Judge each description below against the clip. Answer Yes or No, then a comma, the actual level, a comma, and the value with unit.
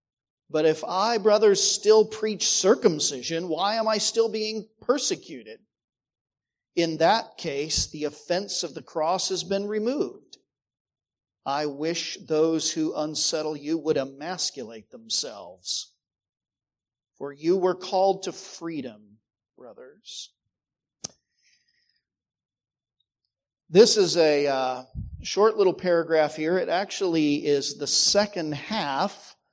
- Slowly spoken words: Yes, slow, 110 wpm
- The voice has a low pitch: No, medium, 165 Hz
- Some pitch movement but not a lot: No, wide, 6.5 semitones